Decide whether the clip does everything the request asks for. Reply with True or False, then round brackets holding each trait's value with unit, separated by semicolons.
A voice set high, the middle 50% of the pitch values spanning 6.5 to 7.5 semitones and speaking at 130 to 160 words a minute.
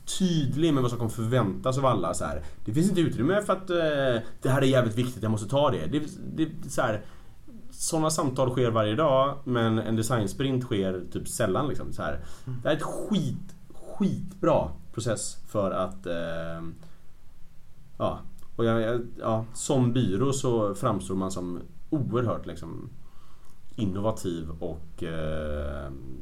False (120 Hz; 7.0 semitones; 155 wpm)